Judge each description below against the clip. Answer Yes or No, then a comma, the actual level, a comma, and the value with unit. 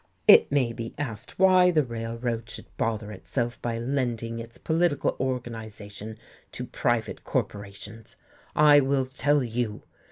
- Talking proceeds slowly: Yes, slow, 130 wpm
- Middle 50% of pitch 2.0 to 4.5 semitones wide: Yes, average, 3.6 semitones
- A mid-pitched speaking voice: No, low, 115 Hz